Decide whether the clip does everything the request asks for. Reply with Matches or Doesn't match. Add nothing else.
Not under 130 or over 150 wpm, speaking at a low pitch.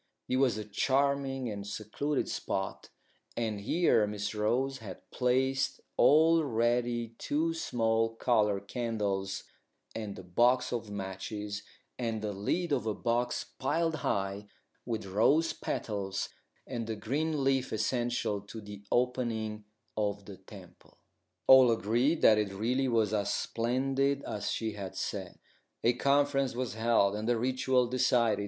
Matches